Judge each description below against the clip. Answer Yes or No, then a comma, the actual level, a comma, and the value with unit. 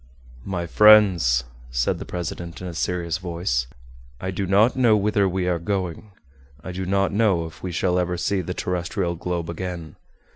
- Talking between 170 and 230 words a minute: Yes, average, 175 wpm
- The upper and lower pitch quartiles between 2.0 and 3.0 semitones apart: Yes, narrow, 2.4 semitones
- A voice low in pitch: Yes, very low, 90 Hz